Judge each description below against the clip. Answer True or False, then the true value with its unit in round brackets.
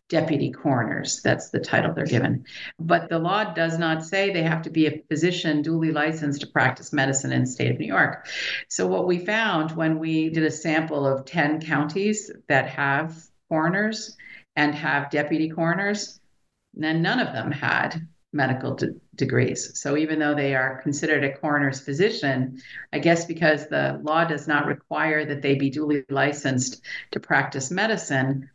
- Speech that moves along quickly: False (170 wpm)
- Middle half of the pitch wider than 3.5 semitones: False (2.9 semitones)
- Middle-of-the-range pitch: True (155 Hz)